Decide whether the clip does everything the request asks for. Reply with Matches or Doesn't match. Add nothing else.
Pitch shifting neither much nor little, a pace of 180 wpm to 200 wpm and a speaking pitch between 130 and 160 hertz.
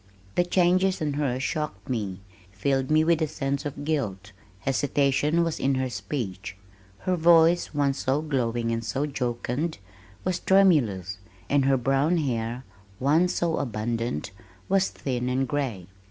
Doesn't match